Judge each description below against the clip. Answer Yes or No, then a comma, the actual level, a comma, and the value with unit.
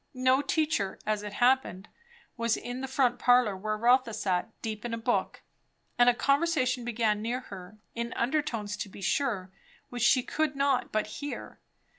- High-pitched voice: Yes, high, 240 Hz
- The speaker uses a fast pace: No, average, 175 wpm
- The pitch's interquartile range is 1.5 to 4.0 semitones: Yes, average, 3.5 semitones